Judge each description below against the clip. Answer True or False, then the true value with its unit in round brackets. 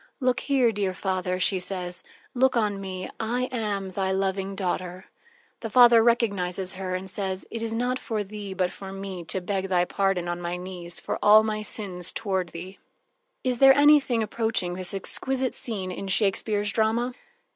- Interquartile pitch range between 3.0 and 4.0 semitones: True (3.4 semitones)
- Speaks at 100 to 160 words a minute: False (175 wpm)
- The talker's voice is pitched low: False (195 Hz)